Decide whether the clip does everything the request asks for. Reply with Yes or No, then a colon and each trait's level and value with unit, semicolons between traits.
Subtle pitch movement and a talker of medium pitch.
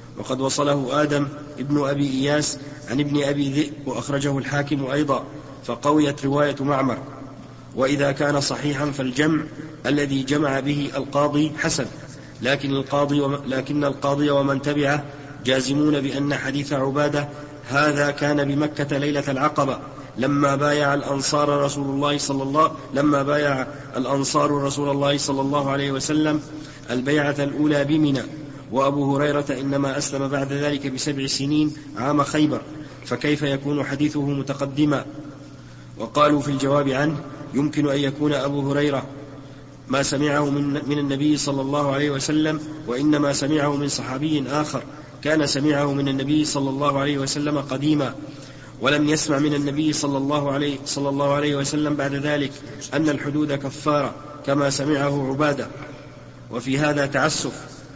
Yes: narrow, 1.1 semitones; medium, 145 Hz